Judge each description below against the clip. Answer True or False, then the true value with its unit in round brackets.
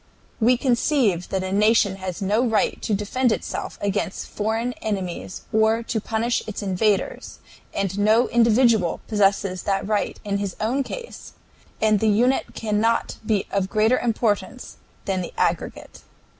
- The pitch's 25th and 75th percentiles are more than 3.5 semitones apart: False (2.6 semitones)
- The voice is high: True (215 Hz)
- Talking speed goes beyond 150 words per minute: False (145 wpm)